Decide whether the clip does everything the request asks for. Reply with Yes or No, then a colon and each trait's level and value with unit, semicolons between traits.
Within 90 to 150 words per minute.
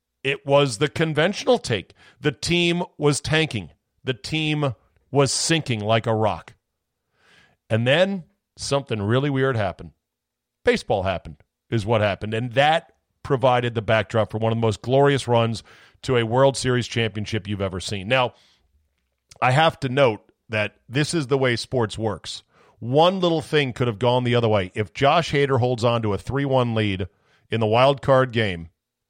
No: average, 170 wpm